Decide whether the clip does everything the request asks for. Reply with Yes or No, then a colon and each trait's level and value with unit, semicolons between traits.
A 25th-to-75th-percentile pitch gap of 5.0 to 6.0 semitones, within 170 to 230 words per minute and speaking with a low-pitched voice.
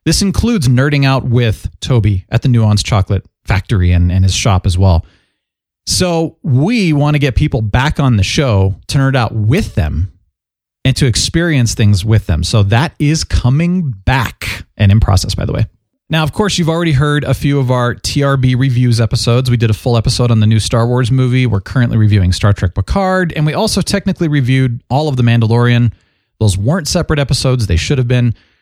Yes: wide, 5.4 semitones; average, 200 wpm; low, 120 Hz